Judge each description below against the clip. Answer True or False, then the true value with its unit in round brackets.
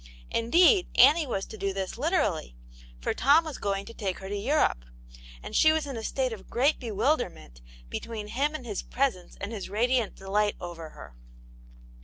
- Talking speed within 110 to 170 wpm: False (180 wpm)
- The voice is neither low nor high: False (225 Hz)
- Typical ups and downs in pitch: False (6.1 semitones)